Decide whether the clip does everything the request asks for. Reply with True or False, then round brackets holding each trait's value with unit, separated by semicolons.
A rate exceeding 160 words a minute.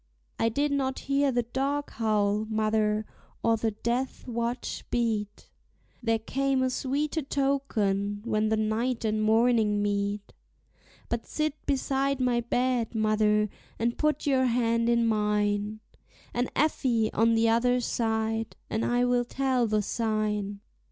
False (140 wpm)